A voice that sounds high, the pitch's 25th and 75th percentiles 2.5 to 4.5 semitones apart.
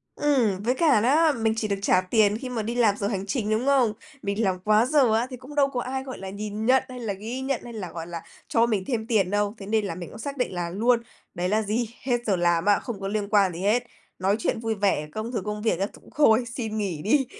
Yes: high, 220 Hz; average, 3.5 semitones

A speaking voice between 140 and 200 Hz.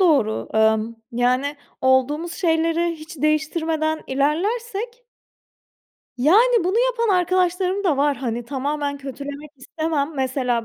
No: very high, 305 Hz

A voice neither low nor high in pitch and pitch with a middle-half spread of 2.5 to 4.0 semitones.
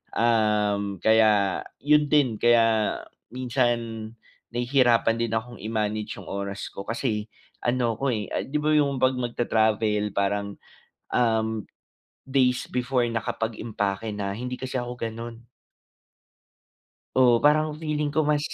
No: low, 115 Hz; average, 3.1 semitones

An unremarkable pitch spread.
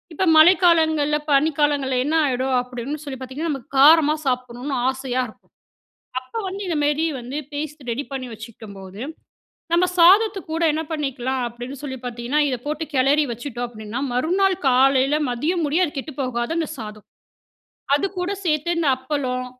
Yes: average, 3.9 semitones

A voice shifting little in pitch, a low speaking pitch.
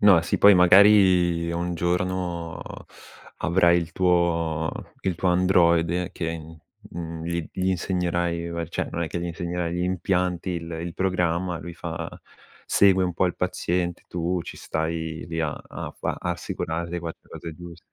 Yes: narrow, 1.3 semitones; very low, 85 Hz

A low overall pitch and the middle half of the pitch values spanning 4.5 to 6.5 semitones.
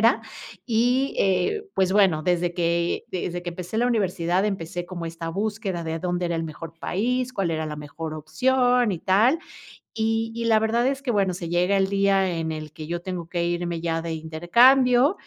No: medium, 180 Hz; average, 5.1 semitones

